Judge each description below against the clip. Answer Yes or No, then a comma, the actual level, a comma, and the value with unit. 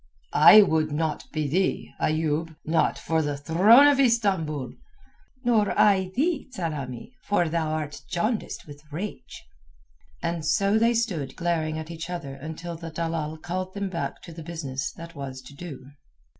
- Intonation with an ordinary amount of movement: Yes, average, 3.8 semitones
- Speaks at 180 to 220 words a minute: No, average, 155 wpm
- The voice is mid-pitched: Yes, medium, 165 Hz